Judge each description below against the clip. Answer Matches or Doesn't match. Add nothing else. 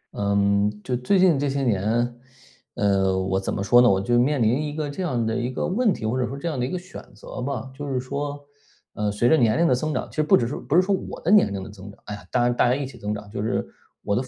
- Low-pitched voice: Matches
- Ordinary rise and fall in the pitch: Doesn't match